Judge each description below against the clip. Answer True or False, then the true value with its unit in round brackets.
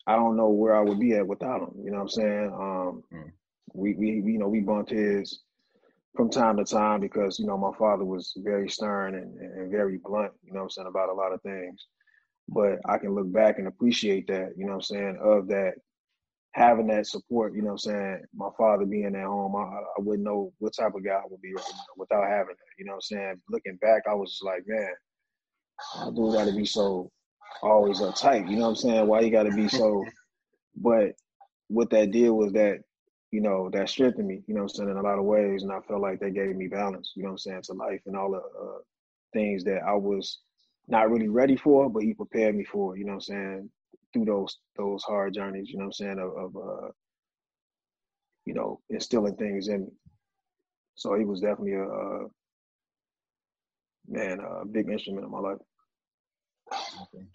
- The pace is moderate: False (220 wpm)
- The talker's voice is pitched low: True (100 Hz)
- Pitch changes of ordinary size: False (1.7 semitones)